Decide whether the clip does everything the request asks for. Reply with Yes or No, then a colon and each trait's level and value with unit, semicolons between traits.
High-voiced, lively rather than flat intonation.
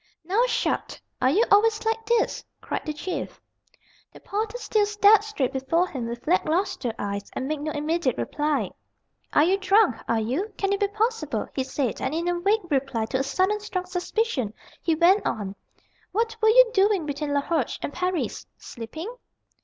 Yes: very high, 350 Hz; wide, 7.1 semitones